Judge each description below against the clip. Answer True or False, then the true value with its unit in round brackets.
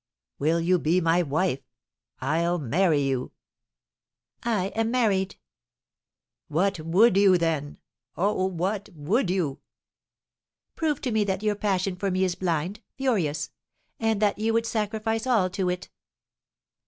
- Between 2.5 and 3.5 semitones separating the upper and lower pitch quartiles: False (4.2 semitones)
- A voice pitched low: False (185 Hz)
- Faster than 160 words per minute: False (135 wpm)